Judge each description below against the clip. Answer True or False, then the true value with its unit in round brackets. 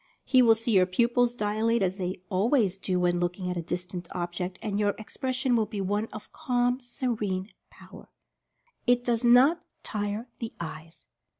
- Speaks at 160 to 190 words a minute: True (175 wpm)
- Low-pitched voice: False (210 Hz)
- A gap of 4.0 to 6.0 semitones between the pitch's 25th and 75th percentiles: True (4.6 semitones)